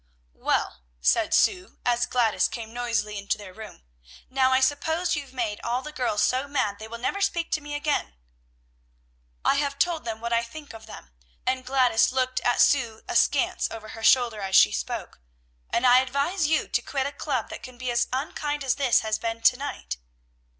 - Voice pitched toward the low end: No, very high, 250 Hz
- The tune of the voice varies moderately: Yes, average, 4.0 semitones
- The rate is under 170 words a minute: No, average, 195 wpm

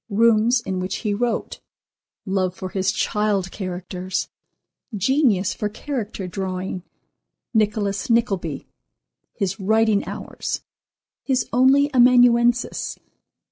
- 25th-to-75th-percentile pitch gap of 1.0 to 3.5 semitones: No, average, 4.0 semitones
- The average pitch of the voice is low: No, high, 210 Hz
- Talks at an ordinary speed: No, slow, 75 wpm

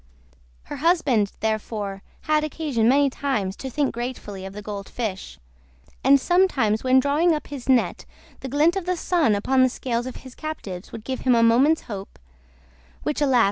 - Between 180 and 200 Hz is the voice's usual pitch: No, very high, 255 Hz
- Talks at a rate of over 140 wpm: Yes, average, 175 wpm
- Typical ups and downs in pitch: No, wide, 5.8 semitones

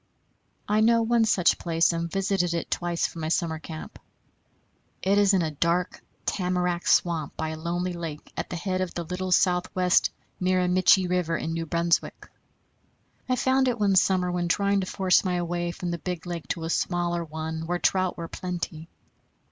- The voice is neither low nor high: Yes, medium, 175 Hz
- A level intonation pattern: Yes, narrow, 1.8 semitones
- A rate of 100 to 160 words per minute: No, average, 185 wpm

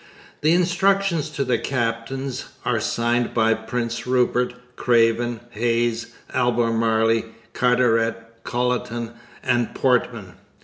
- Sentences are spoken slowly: Yes, slow, 95 wpm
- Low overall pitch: Yes, low, 120 Hz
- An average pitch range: No, narrow, 1.7 semitones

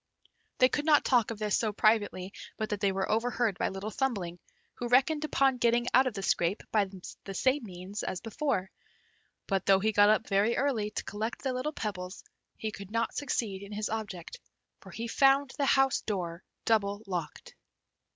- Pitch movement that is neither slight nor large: Yes, average, 4.2 semitones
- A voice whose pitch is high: Yes, high, 215 Hz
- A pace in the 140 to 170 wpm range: No, average, 190 wpm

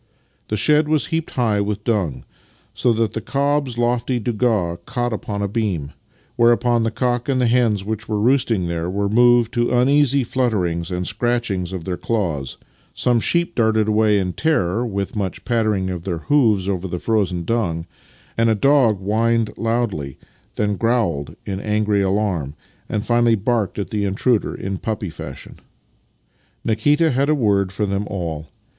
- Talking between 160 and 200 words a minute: Yes, average, 165 wpm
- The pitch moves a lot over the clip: No, average, 3.9 semitones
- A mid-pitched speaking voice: No, low, 110 Hz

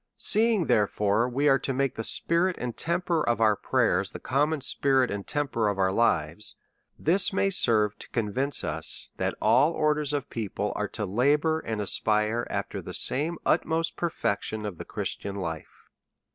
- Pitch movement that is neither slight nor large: No, wide, 6.3 semitones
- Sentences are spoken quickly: No, average, 170 wpm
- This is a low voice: Yes, low, 125 Hz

